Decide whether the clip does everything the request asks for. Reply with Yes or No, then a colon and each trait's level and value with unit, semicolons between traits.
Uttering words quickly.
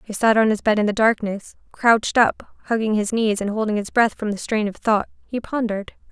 Yes: fast, 235 wpm